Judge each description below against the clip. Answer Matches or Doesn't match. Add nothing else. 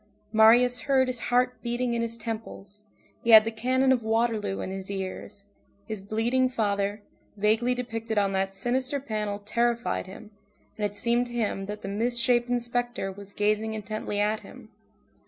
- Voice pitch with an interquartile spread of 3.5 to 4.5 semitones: Doesn't match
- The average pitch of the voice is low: Doesn't match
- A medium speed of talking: Matches